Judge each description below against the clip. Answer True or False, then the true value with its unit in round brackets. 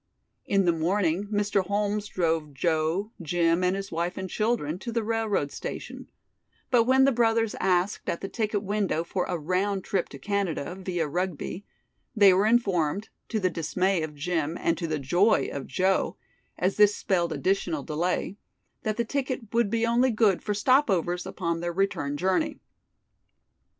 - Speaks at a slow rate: False (170 wpm)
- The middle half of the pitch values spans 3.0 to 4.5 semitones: True (3.7 semitones)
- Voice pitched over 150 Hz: True (190 Hz)